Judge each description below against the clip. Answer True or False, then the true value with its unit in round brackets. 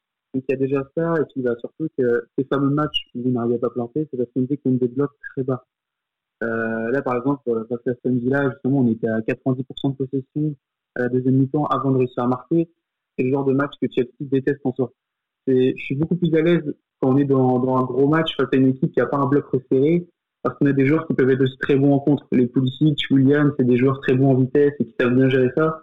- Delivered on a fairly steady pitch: True (2.0 semitones)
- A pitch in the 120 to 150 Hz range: True (135 Hz)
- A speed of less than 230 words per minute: False (270 wpm)